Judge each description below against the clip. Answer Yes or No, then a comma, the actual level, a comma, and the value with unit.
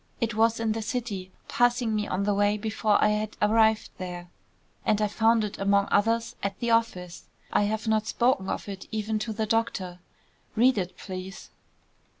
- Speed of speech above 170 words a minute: Yes, average, 180 wpm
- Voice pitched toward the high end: Yes, high, 215 Hz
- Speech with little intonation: Yes, narrow, 2.1 semitones